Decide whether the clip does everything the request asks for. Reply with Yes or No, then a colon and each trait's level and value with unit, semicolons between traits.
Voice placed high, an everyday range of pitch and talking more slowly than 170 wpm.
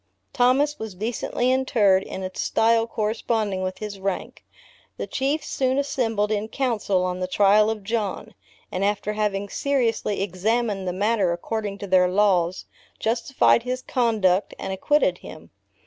Yes: high, 210 Hz; average, 3.4 semitones; average, 145 wpm